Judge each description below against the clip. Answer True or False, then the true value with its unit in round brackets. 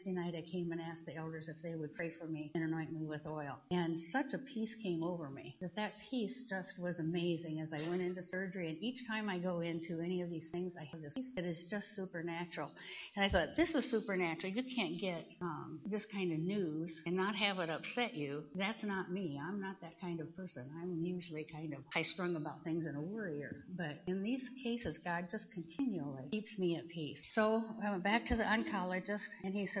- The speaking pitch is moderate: True (175 Hz)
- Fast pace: True (230 wpm)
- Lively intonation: False (3.7 semitones)